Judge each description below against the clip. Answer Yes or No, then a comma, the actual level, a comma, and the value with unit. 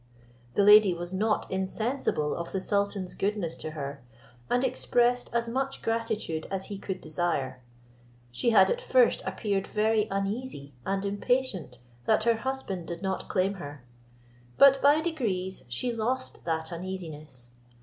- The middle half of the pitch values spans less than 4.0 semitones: No, wide, 5.5 semitones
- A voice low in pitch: No, high, 195 Hz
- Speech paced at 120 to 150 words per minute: Yes, average, 145 wpm